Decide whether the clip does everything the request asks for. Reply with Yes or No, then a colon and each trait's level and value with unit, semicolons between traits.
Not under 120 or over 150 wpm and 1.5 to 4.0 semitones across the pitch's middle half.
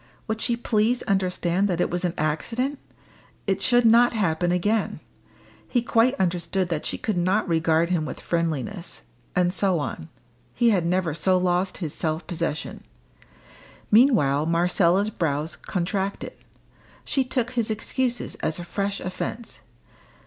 No: average, 140 wpm; average, 4.6 semitones